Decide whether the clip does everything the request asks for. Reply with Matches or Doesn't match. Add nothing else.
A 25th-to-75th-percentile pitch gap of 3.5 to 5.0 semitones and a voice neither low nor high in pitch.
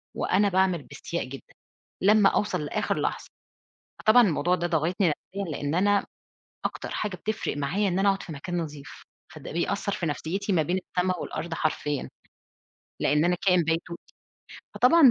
Matches